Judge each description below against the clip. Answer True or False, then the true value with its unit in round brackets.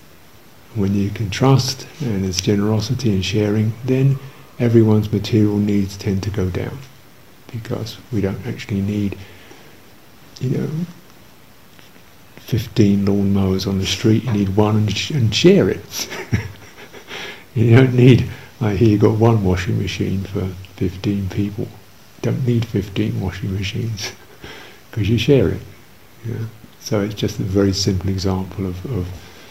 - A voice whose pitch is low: True (105 Hz)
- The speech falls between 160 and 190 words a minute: False (150 wpm)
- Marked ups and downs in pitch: False (3.2 semitones)